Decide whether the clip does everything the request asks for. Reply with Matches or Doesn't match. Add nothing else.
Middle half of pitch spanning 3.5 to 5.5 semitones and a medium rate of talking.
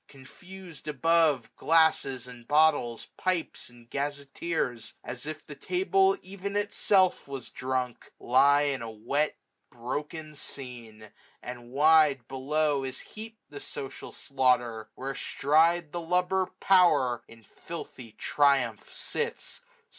Doesn't match